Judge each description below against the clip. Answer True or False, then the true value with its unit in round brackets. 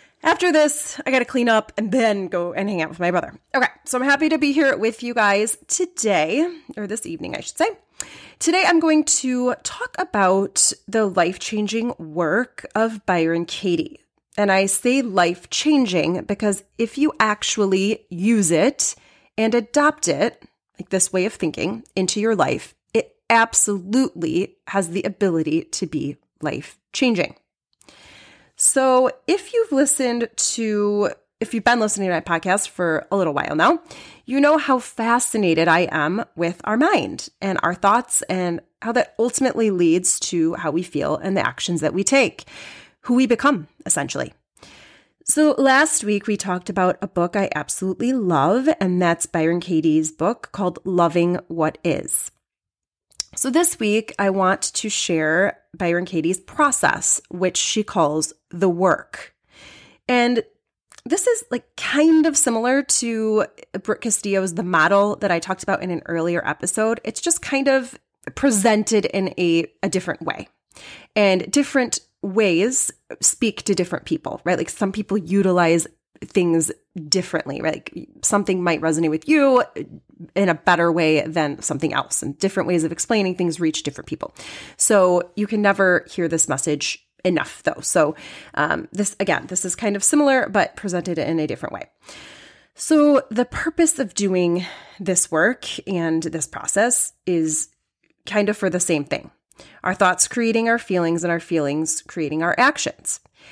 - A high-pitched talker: True (200 Hz)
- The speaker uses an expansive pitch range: True (6.1 semitones)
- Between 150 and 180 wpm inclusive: True (160 wpm)